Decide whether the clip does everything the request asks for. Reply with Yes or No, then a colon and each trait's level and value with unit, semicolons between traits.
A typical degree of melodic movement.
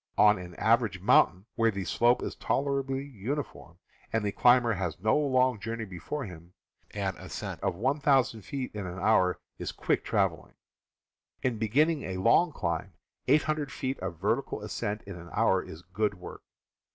No: wide, 5.8 semitones